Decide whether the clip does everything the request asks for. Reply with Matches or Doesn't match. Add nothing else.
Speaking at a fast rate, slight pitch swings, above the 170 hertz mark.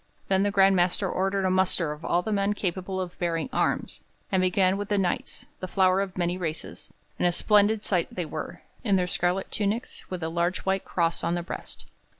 Matches